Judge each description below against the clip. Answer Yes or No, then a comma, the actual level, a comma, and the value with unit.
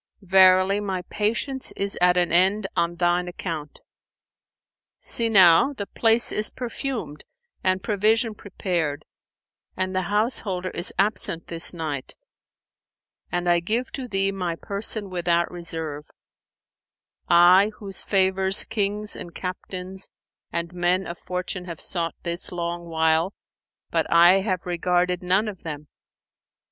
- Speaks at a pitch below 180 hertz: No, medium, 185 Hz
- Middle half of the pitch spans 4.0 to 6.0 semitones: No, average, 2.7 semitones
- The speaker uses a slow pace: Yes, slow, 130 wpm